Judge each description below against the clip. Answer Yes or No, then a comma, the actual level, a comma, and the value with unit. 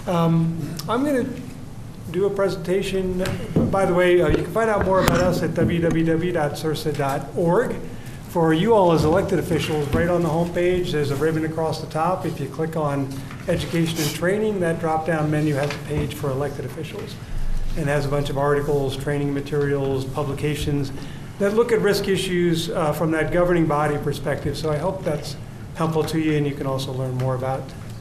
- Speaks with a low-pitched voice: No, medium, 155 Hz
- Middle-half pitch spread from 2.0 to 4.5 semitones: Yes, average, 3.4 semitones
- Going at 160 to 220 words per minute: Yes, average, 185 wpm